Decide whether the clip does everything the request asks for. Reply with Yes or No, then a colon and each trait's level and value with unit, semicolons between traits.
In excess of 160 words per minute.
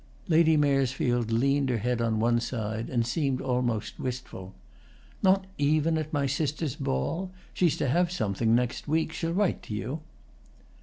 No: average, 155 wpm